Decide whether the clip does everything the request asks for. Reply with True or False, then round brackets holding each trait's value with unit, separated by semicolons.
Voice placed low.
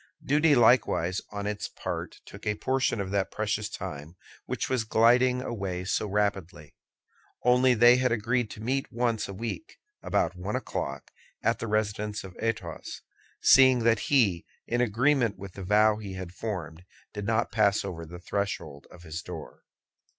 True (105 Hz)